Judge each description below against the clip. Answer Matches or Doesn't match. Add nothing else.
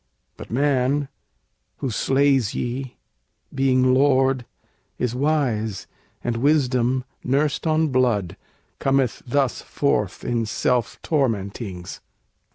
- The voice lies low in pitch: Matches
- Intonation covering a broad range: Doesn't match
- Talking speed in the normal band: Doesn't match